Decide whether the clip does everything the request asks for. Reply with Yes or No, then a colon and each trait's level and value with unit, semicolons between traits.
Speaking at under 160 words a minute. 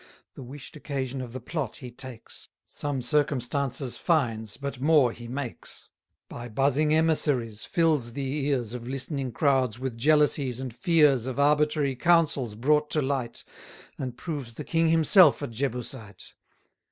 Yes: average, 150 wpm